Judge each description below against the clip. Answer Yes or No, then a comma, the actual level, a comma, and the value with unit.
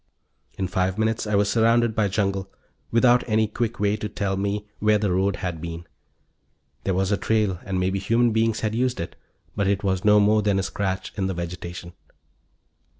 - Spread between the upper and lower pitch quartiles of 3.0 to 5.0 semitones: No, narrow, 2.4 semitones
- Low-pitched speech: Yes, low, 100 Hz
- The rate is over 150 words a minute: Yes, average, 195 wpm